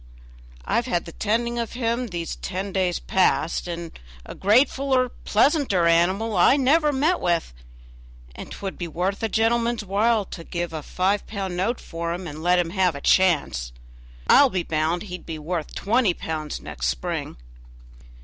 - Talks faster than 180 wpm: No, average, 165 wpm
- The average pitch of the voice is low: No, high, 190 Hz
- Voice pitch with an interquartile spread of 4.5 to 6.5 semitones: Yes, wide, 5.4 semitones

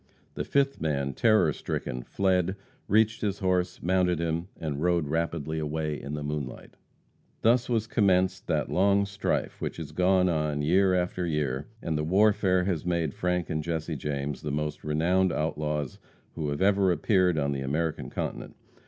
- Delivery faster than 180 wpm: No, average, 165 wpm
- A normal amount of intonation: Yes, average, 3.8 semitones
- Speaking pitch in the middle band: No, very low, 85 Hz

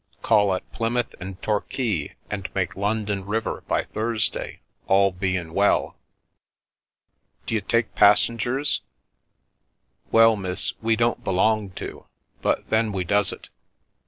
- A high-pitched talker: No, low, 105 Hz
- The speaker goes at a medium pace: No, slow, 130 wpm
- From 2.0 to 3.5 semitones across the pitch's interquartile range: Yes, average, 2.8 semitones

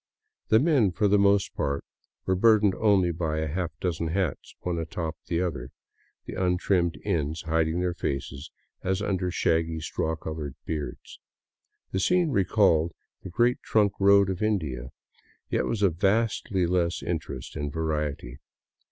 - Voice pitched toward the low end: Yes, very low, 90 Hz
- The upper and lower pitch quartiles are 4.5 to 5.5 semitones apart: No, average, 3.8 semitones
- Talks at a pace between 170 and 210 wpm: No, average, 150 wpm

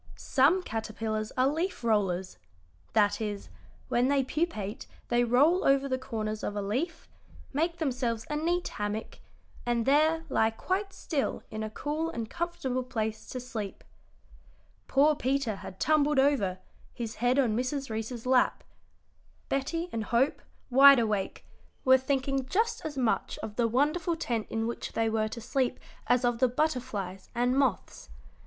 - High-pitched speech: Yes, very high, 250 Hz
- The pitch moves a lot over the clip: No, average, 4.4 semitones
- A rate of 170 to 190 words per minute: No, average, 155 wpm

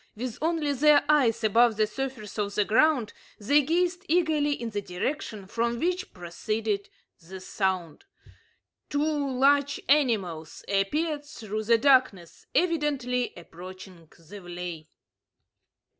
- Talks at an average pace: No, slow, 120 wpm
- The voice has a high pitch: Yes, high, 235 Hz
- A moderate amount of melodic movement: No, wide, 6.9 semitones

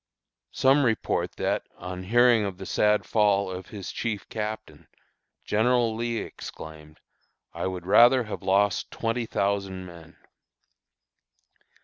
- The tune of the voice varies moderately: Yes, average, 3.7 semitones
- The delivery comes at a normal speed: No, slow, 120 wpm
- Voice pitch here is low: Yes, low, 105 Hz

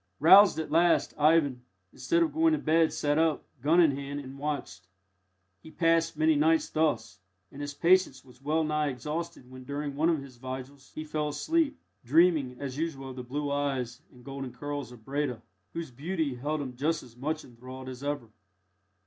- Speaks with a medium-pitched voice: Yes, medium, 145 Hz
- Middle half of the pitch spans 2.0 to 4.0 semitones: Yes, average, 3.6 semitones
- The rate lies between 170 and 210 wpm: Yes, average, 185 wpm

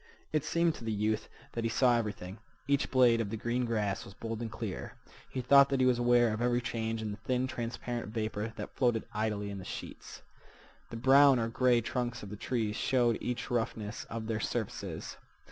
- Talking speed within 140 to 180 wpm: No, average, 200 wpm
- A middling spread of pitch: No, narrow, 2.3 semitones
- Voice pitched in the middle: No, low, 115 Hz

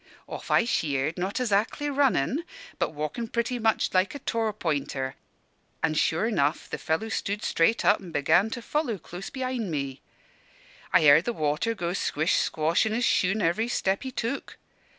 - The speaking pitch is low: No, high, 200 Hz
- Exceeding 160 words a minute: Yes, average, 170 wpm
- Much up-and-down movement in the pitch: Yes, wide, 6.5 semitones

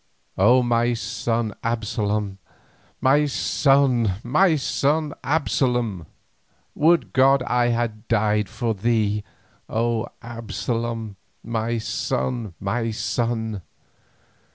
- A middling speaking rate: No, slow, 90 wpm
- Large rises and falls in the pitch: No, narrow, 2.6 semitones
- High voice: No, low, 115 Hz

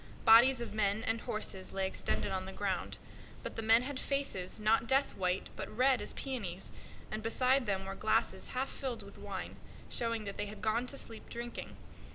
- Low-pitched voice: No, high, 225 Hz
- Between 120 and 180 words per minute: No, average, 195 wpm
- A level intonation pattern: No, average, 4.1 semitones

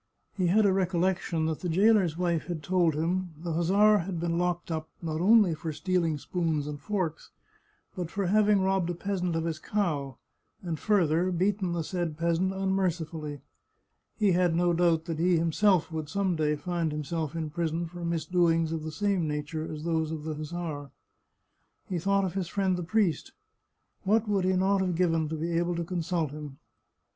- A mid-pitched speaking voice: Yes, medium, 170 Hz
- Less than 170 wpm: No, average, 190 wpm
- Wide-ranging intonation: No, average, 2.7 semitones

